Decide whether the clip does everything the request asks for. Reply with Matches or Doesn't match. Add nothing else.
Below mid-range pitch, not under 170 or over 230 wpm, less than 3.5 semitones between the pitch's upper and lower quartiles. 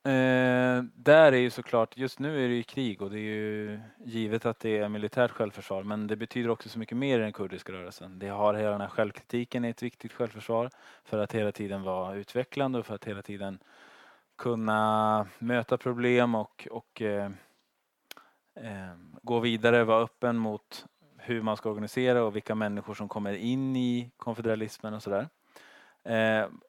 Matches